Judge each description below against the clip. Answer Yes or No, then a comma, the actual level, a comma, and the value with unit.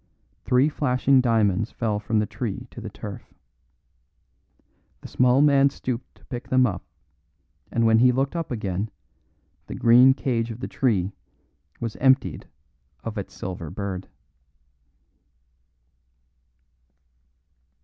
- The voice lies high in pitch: No, low, 115 Hz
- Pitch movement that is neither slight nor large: Yes, average, 3.5 semitones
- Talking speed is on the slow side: Yes, slow, 120 wpm